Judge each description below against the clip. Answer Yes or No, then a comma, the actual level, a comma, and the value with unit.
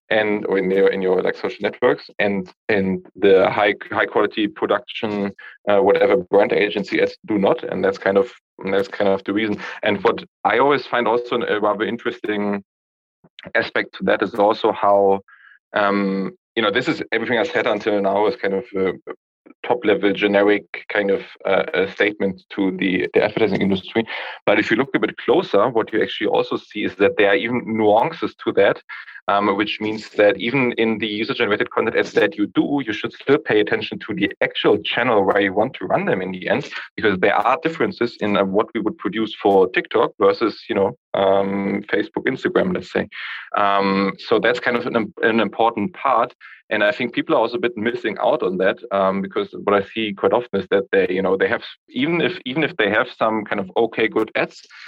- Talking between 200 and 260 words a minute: Yes, fast, 205 wpm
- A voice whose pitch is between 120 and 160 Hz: No, low, 105 Hz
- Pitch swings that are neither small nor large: Yes, average, 3.3 semitones